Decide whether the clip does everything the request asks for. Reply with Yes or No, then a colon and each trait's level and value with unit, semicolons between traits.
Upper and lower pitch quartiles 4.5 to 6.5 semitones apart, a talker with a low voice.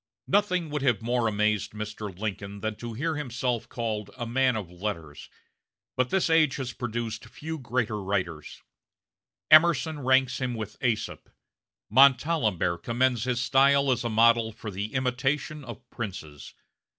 No: average, 3.8 semitones; low, 120 Hz